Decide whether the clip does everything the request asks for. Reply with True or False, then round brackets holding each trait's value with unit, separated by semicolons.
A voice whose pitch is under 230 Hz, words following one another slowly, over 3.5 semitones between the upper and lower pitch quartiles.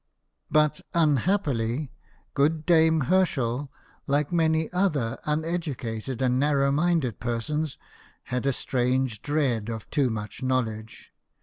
True (140 Hz; 110 wpm; 4.5 semitones)